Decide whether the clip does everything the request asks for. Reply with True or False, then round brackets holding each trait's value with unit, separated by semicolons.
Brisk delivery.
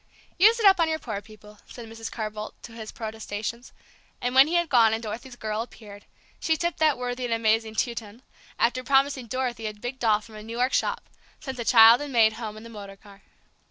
True (230 wpm)